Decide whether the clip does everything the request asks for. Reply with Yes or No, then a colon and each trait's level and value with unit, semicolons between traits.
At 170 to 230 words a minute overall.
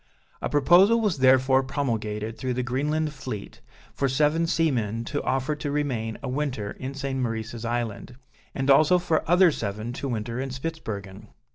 No: average, 160 wpm